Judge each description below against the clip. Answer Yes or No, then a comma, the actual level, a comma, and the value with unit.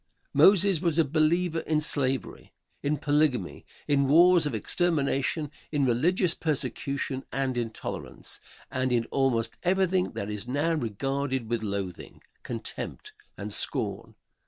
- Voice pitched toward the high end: No, medium, 140 Hz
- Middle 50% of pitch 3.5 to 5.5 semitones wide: Yes, average, 4.7 semitones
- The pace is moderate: No, slow, 125 wpm